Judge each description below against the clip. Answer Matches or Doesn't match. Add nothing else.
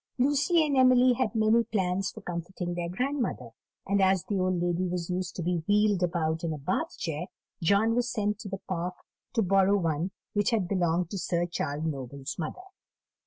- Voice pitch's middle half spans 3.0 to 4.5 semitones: Matches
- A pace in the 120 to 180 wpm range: Doesn't match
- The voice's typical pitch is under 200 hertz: Matches